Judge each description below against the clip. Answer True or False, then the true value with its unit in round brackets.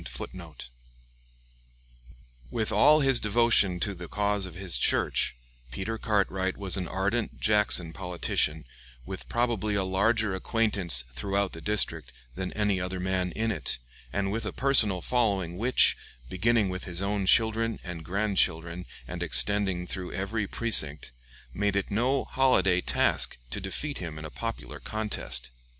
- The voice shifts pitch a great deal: False (3.4 semitones)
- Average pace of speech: True (145 wpm)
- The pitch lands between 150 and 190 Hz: False (100 Hz)